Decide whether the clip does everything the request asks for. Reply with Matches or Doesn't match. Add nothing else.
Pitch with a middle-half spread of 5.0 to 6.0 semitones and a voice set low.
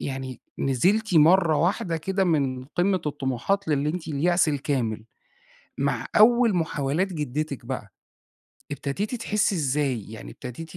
Doesn't match